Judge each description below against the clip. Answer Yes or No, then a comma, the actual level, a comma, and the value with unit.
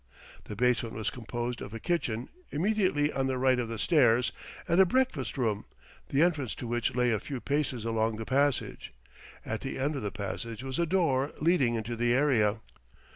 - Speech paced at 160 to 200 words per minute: Yes, average, 190 wpm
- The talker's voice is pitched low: Yes, low, 125 Hz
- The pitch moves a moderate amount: Yes, average, 4.2 semitones